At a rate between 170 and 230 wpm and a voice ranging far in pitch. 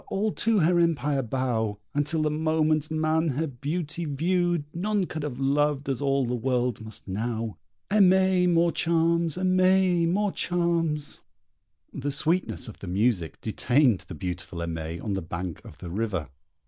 No: average, 150 wpm; wide, 6.8 semitones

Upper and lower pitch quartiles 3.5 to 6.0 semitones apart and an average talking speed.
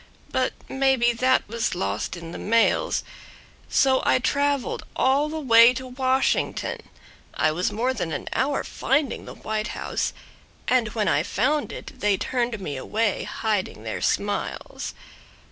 Yes: average, 4.0 semitones; average, 145 wpm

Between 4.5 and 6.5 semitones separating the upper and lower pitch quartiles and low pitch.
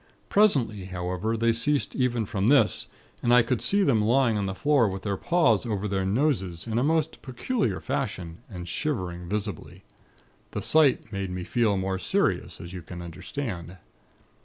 Yes: wide, 5.4 semitones; low, 105 Hz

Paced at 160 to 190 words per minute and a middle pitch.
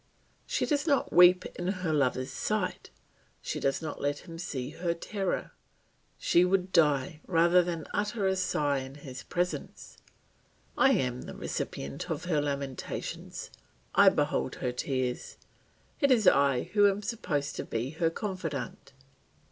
No: average, 150 wpm; medium, 165 Hz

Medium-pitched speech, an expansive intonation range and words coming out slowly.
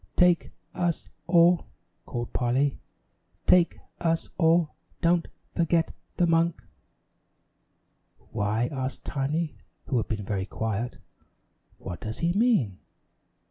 Yes: medium, 155 Hz; wide, 6.3 semitones; slow, 105 wpm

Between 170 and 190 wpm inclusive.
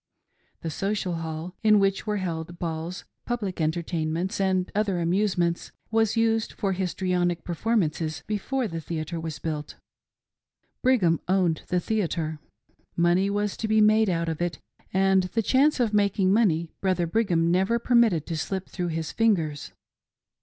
No: average, 155 wpm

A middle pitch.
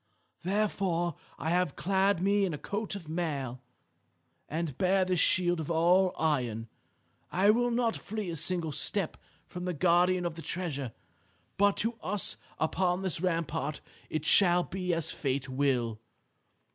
Yes: medium, 175 Hz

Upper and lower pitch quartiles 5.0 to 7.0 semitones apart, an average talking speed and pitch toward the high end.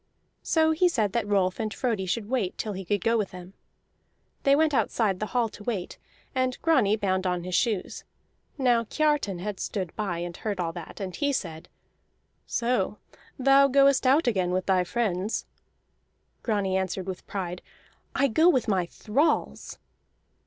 Yes: wide, 5.5 semitones; average, 165 wpm; high, 210 Hz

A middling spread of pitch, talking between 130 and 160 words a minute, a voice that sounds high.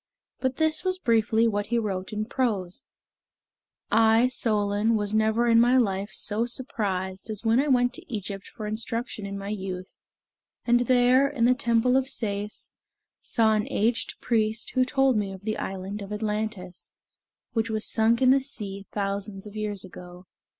No: average, 3.0 semitones; average, 170 wpm; high, 220 Hz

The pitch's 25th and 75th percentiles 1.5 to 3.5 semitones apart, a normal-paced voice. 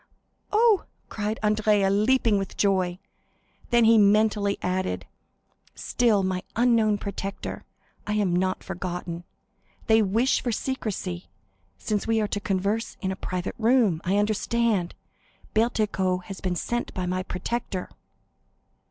No: average, 3.1 semitones; slow, 125 wpm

